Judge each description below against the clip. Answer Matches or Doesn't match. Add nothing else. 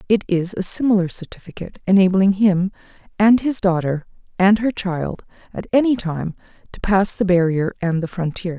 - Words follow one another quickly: Doesn't match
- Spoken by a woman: Matches